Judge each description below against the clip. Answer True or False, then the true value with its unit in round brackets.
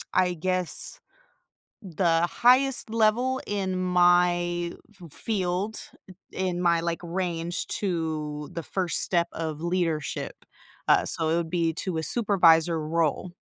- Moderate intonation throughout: False (2.2 semitones)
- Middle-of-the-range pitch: True (175 Hz)